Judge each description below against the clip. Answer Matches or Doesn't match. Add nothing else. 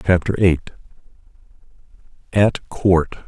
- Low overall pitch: Matches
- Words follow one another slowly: Matches